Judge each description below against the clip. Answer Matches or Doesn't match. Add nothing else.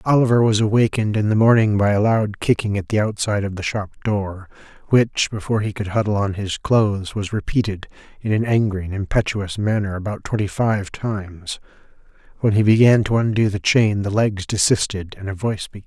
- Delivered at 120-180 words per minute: Doesn't match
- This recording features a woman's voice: Doesn't match